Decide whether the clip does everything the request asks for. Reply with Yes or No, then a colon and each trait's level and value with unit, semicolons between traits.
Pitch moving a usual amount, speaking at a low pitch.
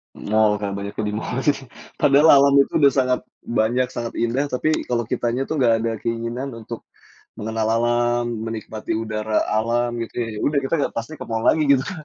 Yes: average, 3.1 semitones; low, 120 Hz